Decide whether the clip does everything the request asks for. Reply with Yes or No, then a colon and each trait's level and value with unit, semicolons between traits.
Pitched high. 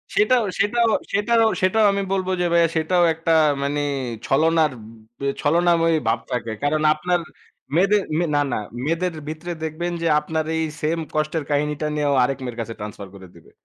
No: medium, 160 Hz